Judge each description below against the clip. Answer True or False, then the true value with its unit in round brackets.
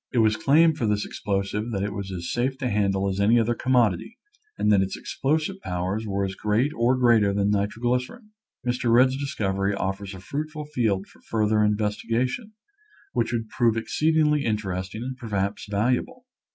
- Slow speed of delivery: False (175 wpm)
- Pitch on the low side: True (110 Hz)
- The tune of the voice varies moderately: True (4.2 semitones)